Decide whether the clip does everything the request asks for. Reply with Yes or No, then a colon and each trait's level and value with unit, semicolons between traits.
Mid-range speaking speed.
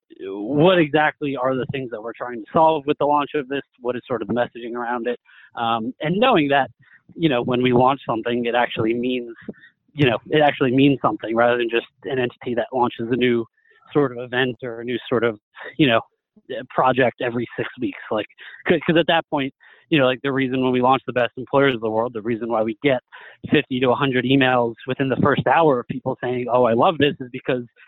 No: fast, 230 wpm